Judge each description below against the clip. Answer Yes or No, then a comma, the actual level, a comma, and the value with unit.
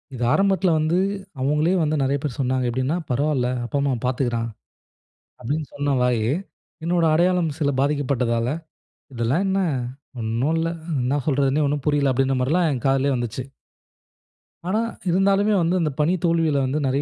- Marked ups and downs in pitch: No, average, 4.1 semitones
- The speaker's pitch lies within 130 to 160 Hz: Yes, medium, 140 Hz